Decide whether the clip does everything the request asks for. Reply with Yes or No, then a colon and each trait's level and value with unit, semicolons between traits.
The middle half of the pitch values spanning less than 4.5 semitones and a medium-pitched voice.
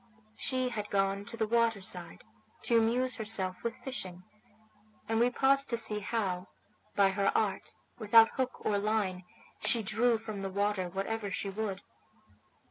No: average, 2.9 semitones; high, 215 Hz